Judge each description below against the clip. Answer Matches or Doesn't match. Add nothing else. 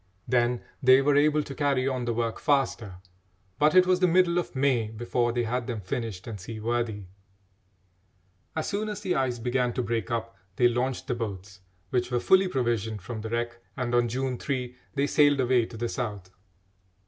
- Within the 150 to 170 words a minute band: Doesn't match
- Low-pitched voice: Matches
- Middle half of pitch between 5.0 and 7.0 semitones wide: Doesn't match